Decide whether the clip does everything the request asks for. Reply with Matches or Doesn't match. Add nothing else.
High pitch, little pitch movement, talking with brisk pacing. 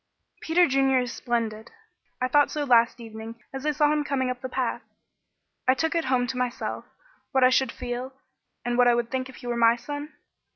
Matches